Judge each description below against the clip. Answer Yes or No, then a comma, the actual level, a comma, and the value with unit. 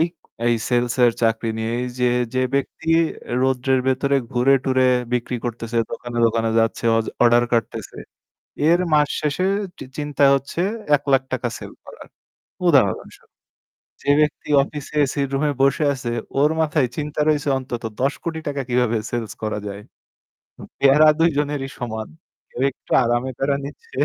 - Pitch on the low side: Yes, low, 130 Hz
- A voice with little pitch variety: No, average, 3.2 semitones